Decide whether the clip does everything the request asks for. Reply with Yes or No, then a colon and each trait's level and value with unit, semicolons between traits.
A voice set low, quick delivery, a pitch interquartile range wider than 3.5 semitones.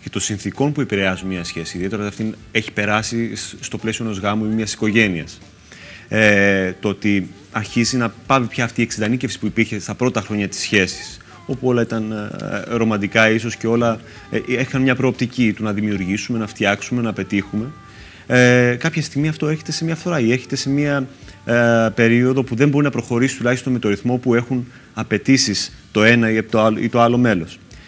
No: low, 110 Hz; fast, 185 wpm; average, 3.2 semitones